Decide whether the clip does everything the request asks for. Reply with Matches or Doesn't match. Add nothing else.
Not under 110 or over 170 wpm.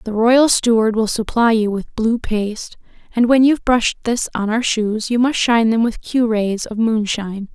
Doesn't match